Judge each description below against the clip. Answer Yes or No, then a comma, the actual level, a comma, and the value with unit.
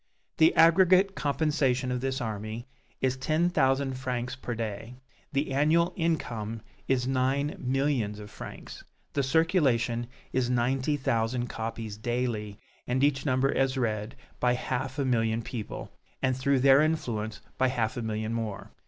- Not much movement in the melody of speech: No, average, 3.2 semitones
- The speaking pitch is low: Yes, low, 130 Hz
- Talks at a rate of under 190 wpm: Yes, average, 145 wpm